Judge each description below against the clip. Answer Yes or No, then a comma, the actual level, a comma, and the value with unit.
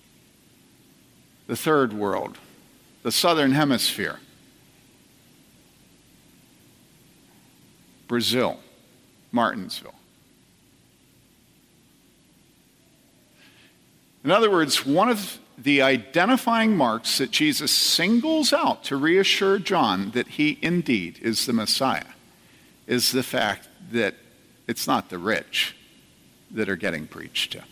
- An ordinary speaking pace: No, slow, 90 wpm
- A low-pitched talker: No, medium, 165 Hz